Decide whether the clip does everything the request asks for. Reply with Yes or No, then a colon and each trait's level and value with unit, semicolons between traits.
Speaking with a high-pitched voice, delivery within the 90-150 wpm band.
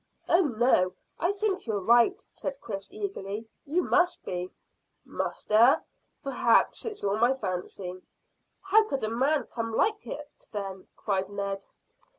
Yes: high, 235 Hz; average, 145 wpm